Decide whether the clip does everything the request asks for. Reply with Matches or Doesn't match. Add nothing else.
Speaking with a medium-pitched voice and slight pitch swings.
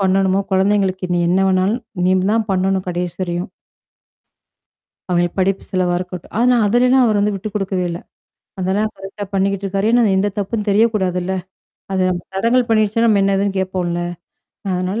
Doesn't match